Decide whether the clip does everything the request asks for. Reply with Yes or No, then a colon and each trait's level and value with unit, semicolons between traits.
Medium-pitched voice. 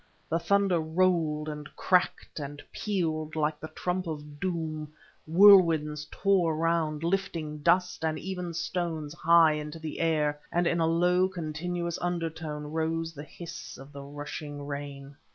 Yes: medium, 160 Hz